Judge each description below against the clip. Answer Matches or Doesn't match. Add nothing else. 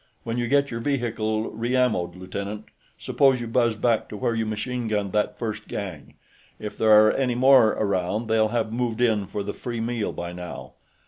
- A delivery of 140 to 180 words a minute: Doesn't match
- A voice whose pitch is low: Matches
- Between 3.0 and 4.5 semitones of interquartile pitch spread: Doesn't match